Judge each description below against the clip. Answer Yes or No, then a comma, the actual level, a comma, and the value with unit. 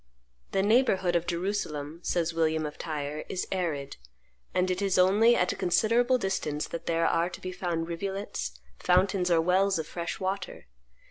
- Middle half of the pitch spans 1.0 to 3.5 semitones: Yes, average, 2.8 semitones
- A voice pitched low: No, medium, 180 Hz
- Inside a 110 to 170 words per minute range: Yes, average, 165 wpm